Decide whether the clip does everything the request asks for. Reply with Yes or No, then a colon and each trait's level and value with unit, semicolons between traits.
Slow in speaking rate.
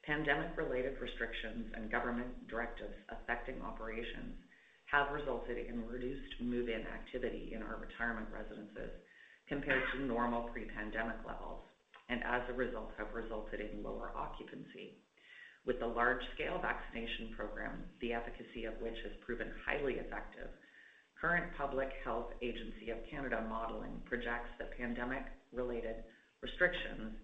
Yes: slow, 130 wpm